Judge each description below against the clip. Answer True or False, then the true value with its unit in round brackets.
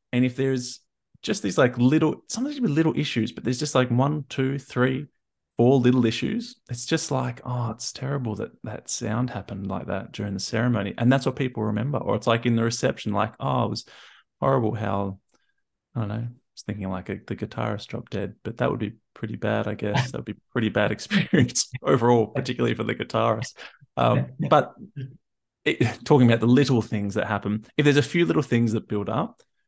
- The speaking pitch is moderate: False (125 Hz)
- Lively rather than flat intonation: False (3.7 semitones)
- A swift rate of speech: True (210 wpm)